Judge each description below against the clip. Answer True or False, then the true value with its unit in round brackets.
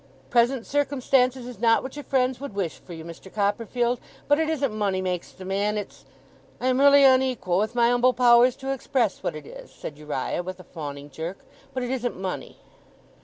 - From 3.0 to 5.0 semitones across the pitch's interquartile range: False (5.6 semitones)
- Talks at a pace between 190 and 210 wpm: True (200 wpm)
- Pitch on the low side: False (235 Hz)